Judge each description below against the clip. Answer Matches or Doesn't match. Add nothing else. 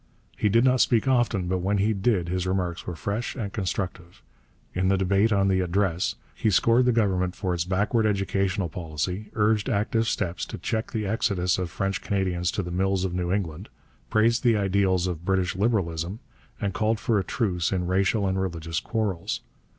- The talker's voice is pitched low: Matches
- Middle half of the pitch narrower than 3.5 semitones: Matches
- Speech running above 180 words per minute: Matches